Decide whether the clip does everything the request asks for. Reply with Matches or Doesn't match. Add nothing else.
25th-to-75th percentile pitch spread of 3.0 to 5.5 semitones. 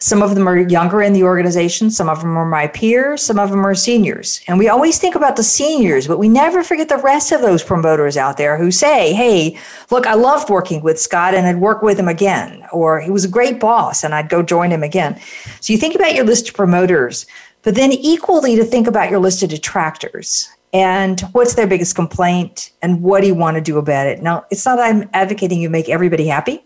Matches